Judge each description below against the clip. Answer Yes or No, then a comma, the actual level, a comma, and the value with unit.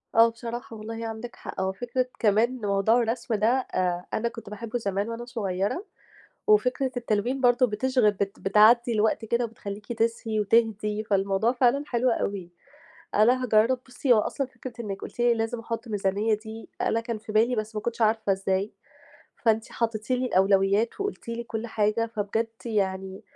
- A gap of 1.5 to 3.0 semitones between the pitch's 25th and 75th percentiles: Yes, narrow, 2.4 semitones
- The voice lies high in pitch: Yes, high, 225 Hz